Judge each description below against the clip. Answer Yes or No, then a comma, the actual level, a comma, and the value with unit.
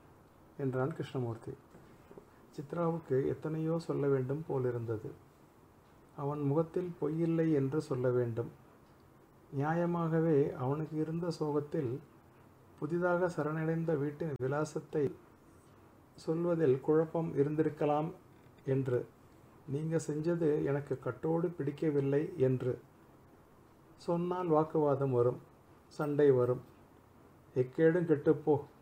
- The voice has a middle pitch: Yes, medium, 150 Hz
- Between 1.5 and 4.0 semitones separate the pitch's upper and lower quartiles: Yes, average, 3.3 semitones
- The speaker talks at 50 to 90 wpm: Yes, average, 80 wpm